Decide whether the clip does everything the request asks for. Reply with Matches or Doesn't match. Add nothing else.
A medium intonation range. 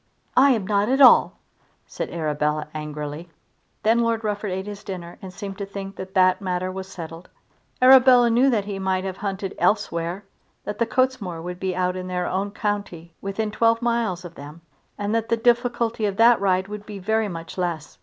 Matches